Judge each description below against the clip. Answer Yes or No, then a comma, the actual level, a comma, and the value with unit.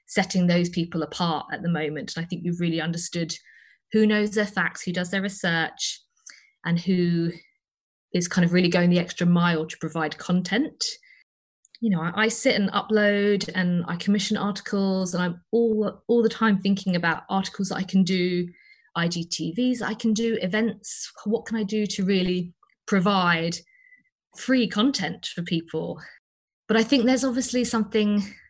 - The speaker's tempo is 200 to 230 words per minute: No, average, 170 wpm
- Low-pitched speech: No, high, 195 Hz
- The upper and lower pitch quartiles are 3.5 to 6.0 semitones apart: Yes, average, 3.9 semitones